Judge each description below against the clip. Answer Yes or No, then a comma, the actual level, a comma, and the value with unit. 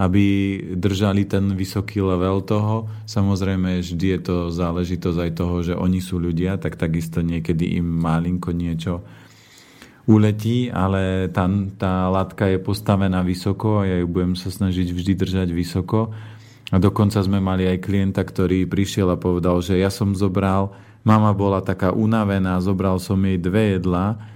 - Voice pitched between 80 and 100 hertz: Yes, very low, 95 Hz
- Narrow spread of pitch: Yes, narrow, 1.8 semitones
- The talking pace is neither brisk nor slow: Yes, average, 155 wpm